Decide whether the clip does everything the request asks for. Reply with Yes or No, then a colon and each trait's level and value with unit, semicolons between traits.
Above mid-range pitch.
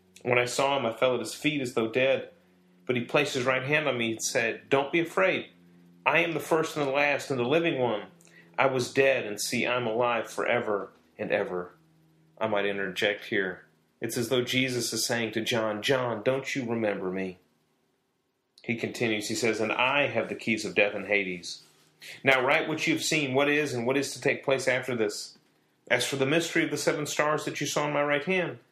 No: low, 125 Hz